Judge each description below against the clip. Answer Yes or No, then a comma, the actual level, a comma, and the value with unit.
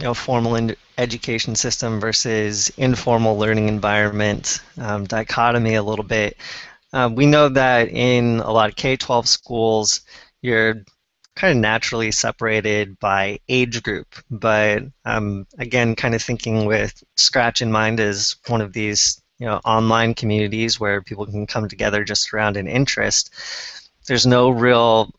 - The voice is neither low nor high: No, low, 110 Hz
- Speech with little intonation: Yes, narrow, 2.3 semitones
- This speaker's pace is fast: No, average, 150 wpm